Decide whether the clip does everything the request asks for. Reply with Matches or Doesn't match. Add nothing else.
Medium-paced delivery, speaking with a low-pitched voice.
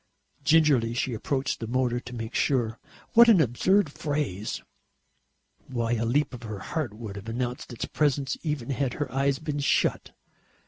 Matches